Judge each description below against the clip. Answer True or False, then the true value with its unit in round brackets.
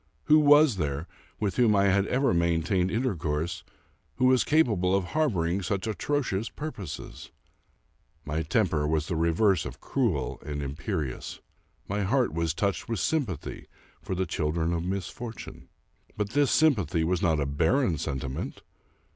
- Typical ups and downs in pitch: False (6.3 semitones)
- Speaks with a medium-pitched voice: False (95 Hz)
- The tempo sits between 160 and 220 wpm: False (145 wpm)